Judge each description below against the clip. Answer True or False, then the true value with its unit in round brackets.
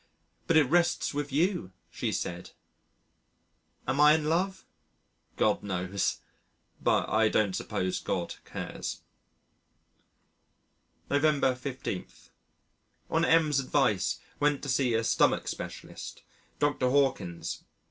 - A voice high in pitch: False (135 Hz)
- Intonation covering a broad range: True (5.8 semitones)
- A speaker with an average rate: False (110 wpm)